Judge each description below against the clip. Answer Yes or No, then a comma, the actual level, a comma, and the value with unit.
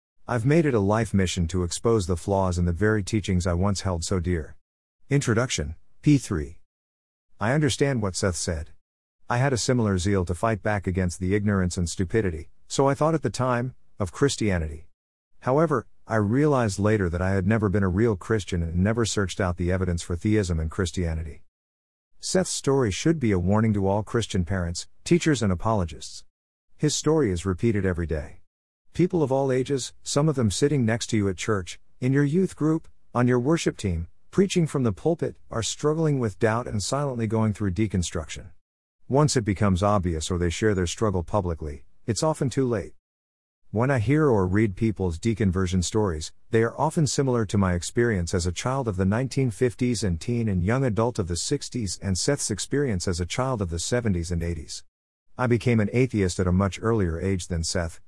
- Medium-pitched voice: No, low, 100 Hz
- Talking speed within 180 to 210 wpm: Yes, average, 195 wpm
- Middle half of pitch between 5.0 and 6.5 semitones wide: Yes, wide, 5.4 semitones